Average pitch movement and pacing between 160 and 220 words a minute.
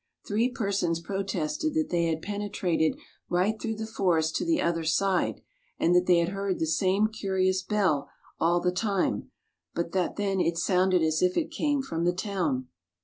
Yes: average, 3.3 semitones; average, 180 wpm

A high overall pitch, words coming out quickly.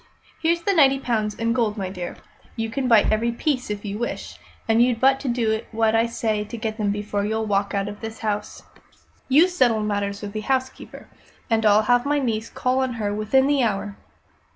Yes: high, 225 Hz; fast, 210 wpm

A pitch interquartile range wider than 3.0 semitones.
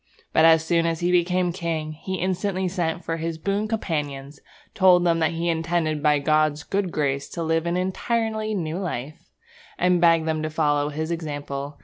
No: average, 2.7 semitones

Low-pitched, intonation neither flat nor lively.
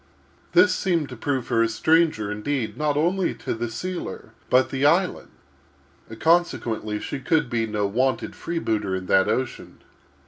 No: low, 130 Hz; wide, 6.4 semitones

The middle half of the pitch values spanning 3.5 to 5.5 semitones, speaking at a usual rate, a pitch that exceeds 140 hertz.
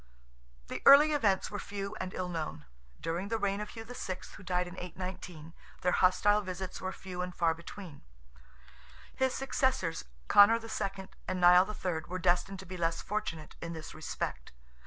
No: average, 2.7 semitones; average, 170 wpm; medium, 185 Hz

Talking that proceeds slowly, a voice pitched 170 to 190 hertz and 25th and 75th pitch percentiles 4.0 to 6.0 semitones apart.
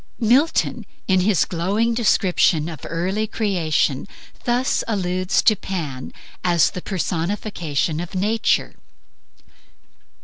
Yes: slow, 105 wpm; medium, 185 Hz; average, 4.3 semitones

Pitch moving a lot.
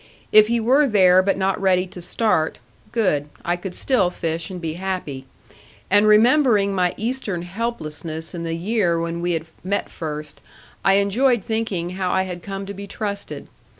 No: average, 3.7 semitones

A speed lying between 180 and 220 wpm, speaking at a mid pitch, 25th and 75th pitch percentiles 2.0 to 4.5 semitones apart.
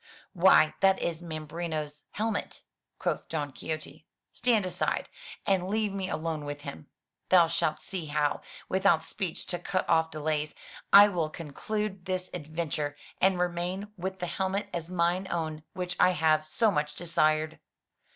No: average, 150 wpm; medium, 170 Hz; average, 3.4 semitones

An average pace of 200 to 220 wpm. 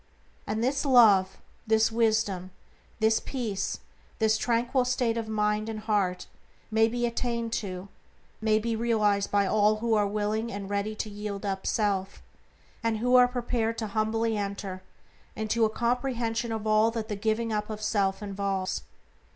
No: average, 160 wpm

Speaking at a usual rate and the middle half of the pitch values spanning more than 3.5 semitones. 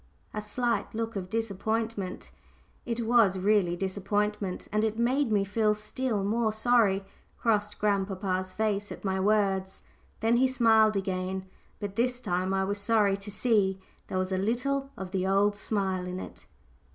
No: average, 160 wpm; average, 2.7 semitones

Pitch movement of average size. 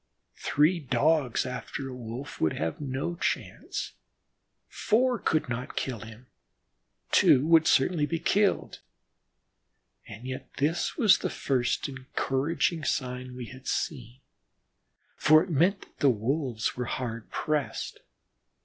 Yes: average, 4.2 semitones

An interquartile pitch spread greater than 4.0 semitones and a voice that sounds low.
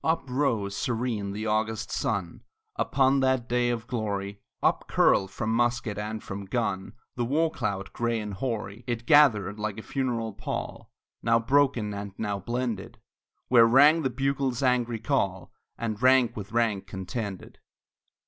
No: average, 3.6 semitones; low, 115 Hz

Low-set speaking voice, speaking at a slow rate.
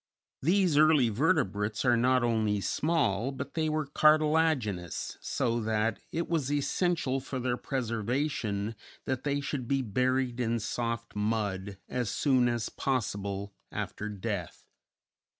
Yes: low, 125 Hz; slow, 130 wpm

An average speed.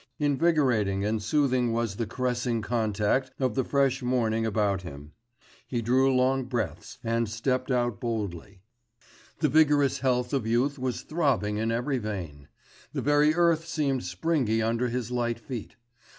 Yes: average, 150 wpm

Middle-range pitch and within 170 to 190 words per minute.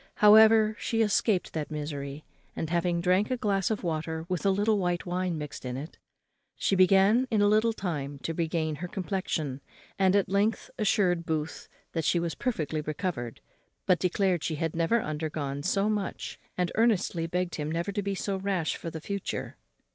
Yes: medium, 180 Hz; average, 180 wpm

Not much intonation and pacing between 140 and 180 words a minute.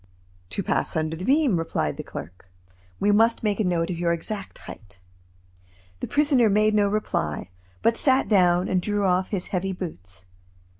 No: average, 4.2 semitones; average, 170 wpm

